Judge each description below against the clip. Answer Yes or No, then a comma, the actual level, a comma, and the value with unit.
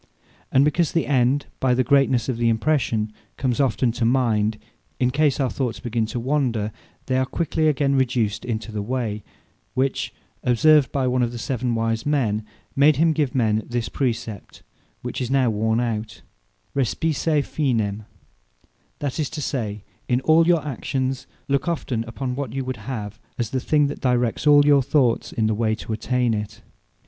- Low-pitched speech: Yes, low, 125 Hz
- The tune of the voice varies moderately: Yes, average, 3.5 semitones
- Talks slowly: No, average, 175 wpm